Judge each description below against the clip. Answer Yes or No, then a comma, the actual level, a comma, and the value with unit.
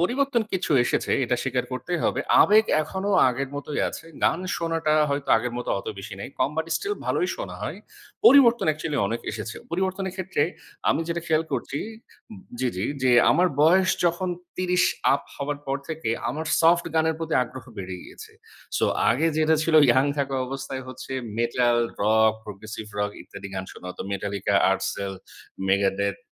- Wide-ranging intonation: Yes, wide, 6.8 semitones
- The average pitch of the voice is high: No, medium, 140 Hz